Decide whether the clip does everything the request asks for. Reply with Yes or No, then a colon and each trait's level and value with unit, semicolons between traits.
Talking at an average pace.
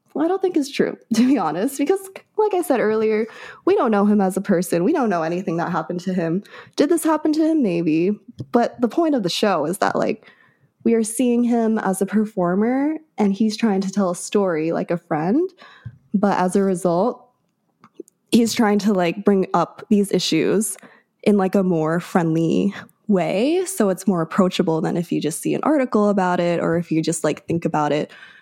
No: fast, 210 wpm